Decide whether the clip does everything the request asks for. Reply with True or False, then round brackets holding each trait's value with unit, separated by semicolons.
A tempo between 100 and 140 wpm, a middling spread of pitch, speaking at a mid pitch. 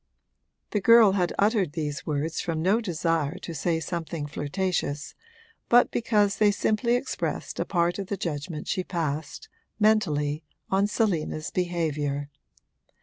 True (135 wpm; 4.9 semitones; 175 Hz)